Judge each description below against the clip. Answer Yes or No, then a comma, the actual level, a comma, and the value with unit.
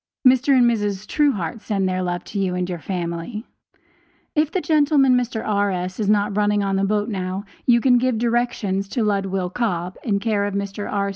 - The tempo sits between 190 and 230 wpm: Yes, average, 195 wpm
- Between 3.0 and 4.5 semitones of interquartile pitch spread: Yes, average, 3.8 semitones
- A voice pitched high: Yes, high, 205 Hz